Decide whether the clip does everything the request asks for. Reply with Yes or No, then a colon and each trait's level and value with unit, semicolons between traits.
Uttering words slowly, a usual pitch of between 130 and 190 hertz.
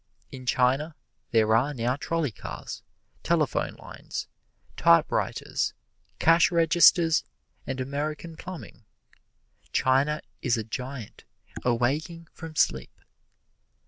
Yes: slow, 95 wpm; medium, 140 Hz